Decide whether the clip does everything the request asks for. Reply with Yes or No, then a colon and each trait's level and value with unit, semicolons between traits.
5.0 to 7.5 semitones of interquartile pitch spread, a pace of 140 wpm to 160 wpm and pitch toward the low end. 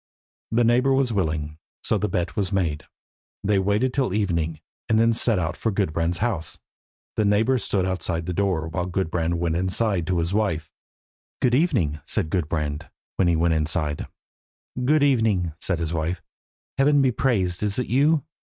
No: wide, 5.4 semitones; average, 170 wpm; very low, 95 Hz